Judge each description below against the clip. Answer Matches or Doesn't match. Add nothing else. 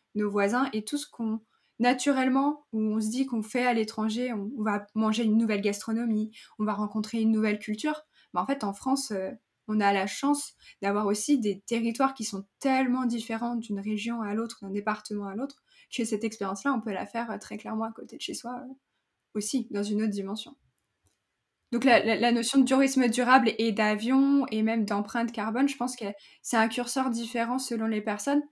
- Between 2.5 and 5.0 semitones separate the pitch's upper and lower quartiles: Matches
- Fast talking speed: Doesn't match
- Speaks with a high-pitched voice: Matches